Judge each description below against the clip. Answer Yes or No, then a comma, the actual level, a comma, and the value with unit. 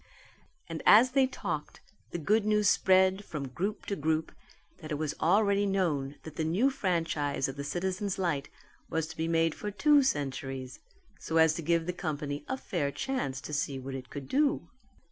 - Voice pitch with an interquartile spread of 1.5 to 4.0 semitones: No, wide, 5.6 semitones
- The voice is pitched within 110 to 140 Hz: No, medium, 165 Hz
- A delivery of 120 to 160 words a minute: No, average, 185 wpm